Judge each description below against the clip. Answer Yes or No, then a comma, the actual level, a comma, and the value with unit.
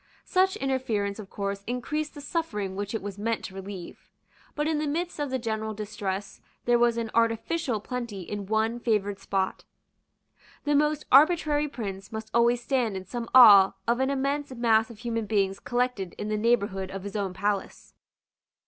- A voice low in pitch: No, high, 225 Hz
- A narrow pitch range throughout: No, average, 4.5 semitones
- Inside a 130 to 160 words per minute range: No, average, 175 wpm